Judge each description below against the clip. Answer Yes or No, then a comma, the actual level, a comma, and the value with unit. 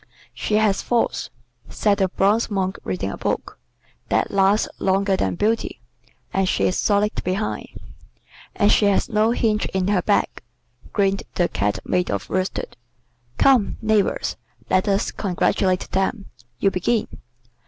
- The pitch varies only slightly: Yes, narrow, 2.1 semitones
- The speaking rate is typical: Yes, average, 145 wpm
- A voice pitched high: Yes, high, 195 Hz